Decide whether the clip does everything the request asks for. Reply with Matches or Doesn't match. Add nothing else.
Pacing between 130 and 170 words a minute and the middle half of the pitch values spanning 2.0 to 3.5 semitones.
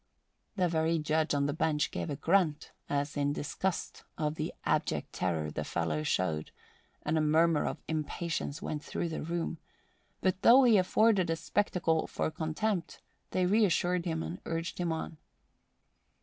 Matches